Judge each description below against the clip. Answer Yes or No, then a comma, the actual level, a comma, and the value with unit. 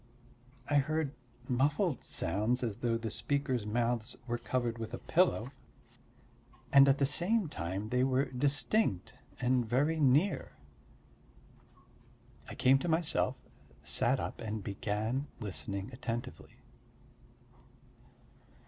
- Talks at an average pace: No, slow, 110 wpm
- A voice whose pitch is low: Yes, low, 125 Hz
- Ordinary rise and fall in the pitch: Yes, average, 4.1 semitones